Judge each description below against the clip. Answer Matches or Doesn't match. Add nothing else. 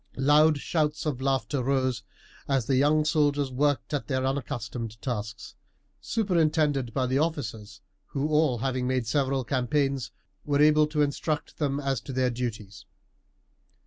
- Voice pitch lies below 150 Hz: Matches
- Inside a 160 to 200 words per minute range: Doesn't match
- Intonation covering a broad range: Doesn't match